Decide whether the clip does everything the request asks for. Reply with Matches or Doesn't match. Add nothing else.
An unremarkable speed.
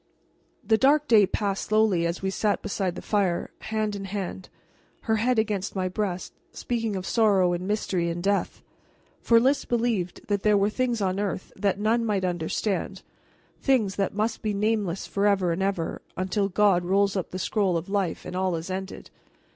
Matches